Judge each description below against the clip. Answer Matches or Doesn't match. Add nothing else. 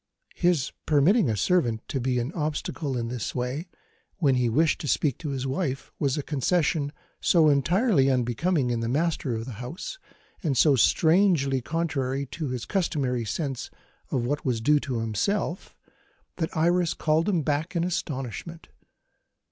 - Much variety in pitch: Doesn't match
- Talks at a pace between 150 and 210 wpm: Matches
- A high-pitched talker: Doesn't match